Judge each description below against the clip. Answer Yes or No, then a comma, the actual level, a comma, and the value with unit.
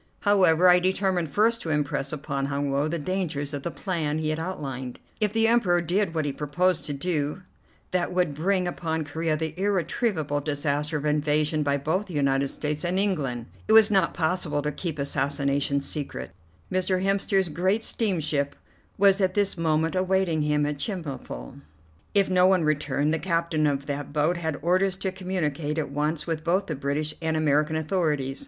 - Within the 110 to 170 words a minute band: No, average, 180 wpm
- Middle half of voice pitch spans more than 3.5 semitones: Yes, average, 4.0 semitones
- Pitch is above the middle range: No, medium, 160 Hz